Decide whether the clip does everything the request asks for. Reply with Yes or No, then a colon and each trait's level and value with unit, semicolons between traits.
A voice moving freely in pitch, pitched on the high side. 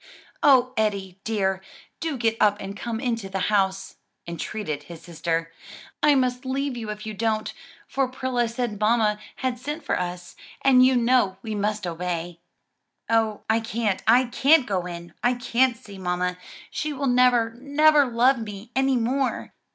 No: average, 4.7 semitones; high, 225 Hz